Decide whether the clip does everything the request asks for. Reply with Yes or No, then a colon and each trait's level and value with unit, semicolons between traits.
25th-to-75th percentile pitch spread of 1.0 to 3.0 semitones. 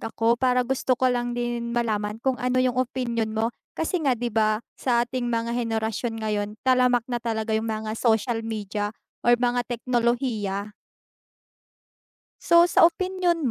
Yes: narrow, 2.4 semitones